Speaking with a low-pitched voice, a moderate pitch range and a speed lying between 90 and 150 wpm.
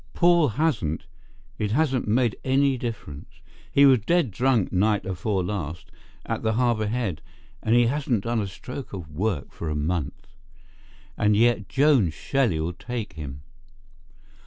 No: low, 110 Hz; wide, 6.0 semitones; average, 145 wpm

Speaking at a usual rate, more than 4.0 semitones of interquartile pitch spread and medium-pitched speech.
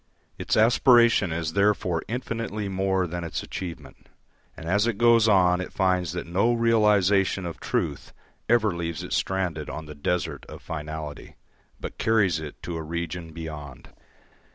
No: average, 155 wpm; average, 4.4 semitones; very low, 90 Hz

